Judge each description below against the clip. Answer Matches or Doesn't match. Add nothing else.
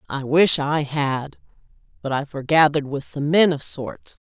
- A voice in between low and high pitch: Matches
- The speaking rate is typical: Matches